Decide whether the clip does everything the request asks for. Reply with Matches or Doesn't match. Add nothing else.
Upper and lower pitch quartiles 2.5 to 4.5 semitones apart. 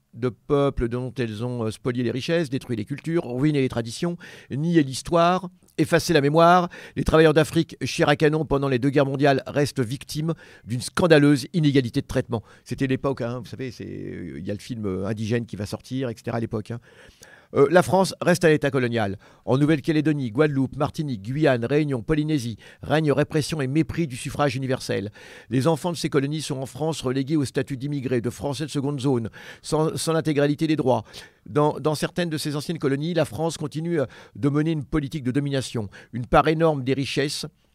Matches